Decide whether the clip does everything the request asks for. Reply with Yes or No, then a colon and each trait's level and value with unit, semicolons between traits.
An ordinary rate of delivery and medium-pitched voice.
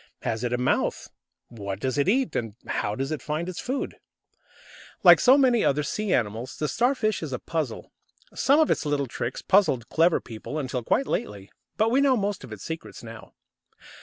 Yes: average, 195 wpm; medium, 150 Hz